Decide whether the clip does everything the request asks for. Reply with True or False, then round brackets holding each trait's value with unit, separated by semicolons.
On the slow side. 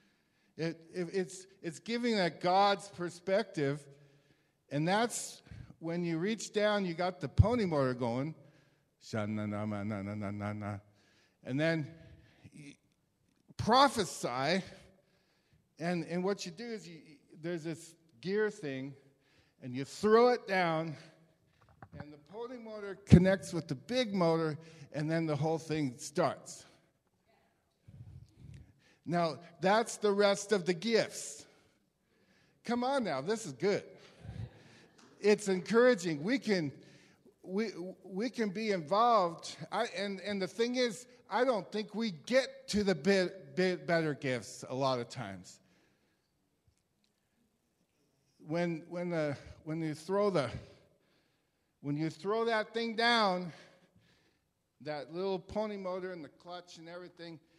True (125 wpm)